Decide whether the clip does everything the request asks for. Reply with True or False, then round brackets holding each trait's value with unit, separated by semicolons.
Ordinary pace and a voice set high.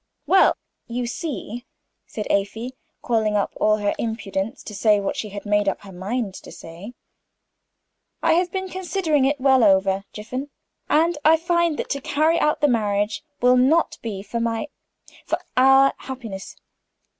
True (160 wpm; 240 Hz)